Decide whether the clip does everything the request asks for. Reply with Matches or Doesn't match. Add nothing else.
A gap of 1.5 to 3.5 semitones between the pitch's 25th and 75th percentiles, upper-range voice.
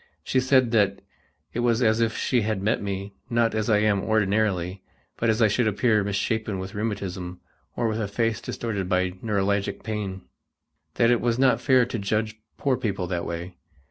Doesn't match